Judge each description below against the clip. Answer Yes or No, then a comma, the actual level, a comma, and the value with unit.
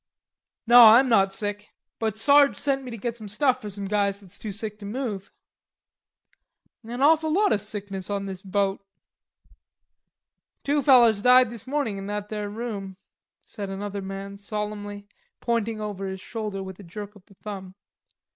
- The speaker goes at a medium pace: Yes, average, 165 wpm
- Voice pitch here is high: Yes, high, 210 Hz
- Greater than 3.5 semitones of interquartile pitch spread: No, average, 2.9 semitones